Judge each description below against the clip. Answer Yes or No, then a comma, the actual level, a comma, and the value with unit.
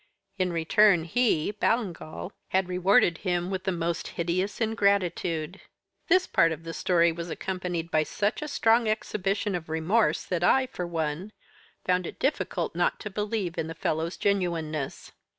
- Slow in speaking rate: No, average, 155 wpm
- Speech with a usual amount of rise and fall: Yes, average, 3.7 semitones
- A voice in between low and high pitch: Yes, medium, 180 Hz